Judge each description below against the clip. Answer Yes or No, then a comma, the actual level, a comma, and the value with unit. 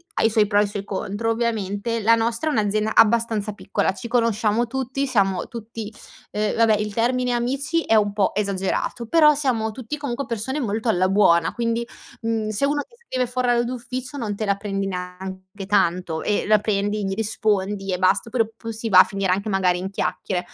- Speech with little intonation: No, average, 3.1 semitones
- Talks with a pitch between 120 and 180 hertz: No, high, 215 Hz